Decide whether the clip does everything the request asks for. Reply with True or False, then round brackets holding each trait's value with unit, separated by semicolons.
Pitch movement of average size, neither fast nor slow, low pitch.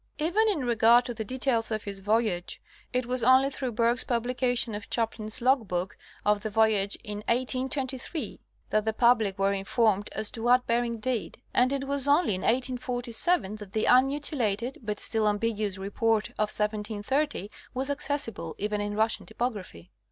False (3.4 semitones; 160 wpm; 230 Hz)